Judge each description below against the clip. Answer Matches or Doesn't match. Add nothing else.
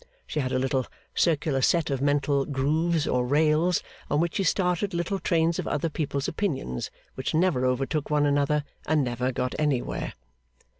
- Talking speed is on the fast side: Doesn't match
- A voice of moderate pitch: Matches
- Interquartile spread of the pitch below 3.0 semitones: Doesn't match